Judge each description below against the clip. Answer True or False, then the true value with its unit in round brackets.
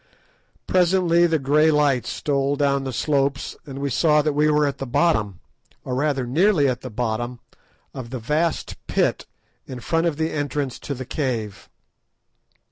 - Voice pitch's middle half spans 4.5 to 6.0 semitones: False (3.1 semitones)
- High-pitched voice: False (140 Hz)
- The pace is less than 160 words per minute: False (165 wpm)